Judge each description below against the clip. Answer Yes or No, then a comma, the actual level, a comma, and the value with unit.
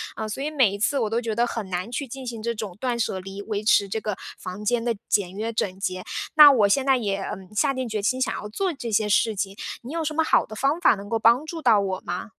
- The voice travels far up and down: No, average, 4.2 semitones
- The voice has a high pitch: Yes, high, 220 Hz